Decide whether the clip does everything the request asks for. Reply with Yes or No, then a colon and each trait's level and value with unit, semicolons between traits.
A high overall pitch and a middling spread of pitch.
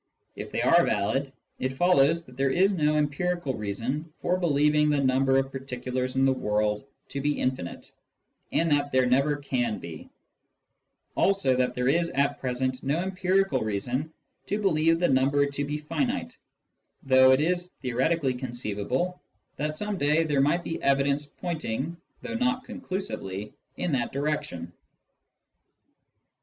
No: medium, 140 Hz; average, 4.3 semitones